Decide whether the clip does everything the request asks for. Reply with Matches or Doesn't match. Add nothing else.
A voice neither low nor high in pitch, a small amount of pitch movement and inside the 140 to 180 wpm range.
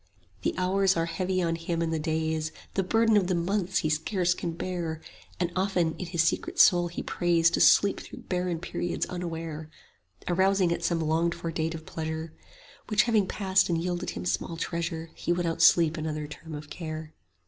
Doesn't match